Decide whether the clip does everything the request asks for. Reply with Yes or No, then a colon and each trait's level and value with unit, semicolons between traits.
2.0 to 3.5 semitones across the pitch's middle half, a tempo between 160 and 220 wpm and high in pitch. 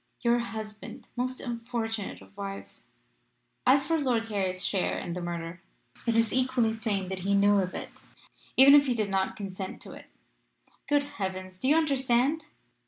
No: average, 4.8 semitones; average, 170 wpm; high, 225 Hz